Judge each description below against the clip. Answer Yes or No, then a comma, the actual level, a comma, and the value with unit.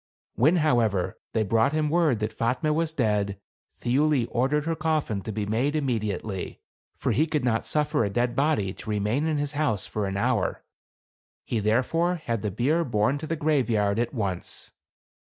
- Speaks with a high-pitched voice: No, low, 120 Hz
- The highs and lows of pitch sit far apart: Yes, wide, 6.0 semitones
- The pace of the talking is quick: No, average, 175 wpm